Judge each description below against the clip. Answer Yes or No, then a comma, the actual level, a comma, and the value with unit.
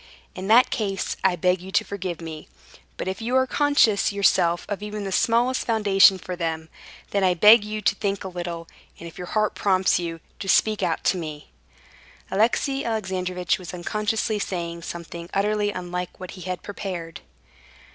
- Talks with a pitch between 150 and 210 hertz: Yes, high, 190 Hz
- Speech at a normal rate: Yes, average, 175 wpm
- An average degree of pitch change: Yes, average, 3.2 semitones